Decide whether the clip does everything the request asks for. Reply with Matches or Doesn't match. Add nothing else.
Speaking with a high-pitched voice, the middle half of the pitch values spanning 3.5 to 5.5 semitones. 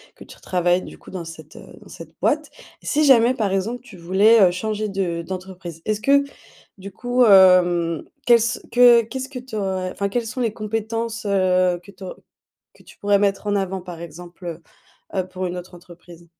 Matches